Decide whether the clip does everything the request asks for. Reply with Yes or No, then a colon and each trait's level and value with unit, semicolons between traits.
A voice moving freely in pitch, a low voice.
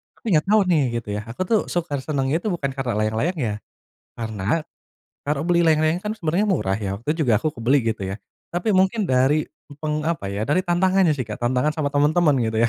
No: wide, 6.3 semitones; medium, 150 Hz